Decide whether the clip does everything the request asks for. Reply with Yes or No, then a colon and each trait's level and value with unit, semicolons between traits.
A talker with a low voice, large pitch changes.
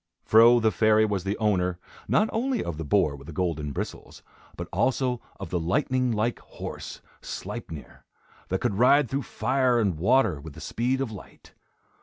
Yes: low, 110 Hz; wide, 6.4 semitones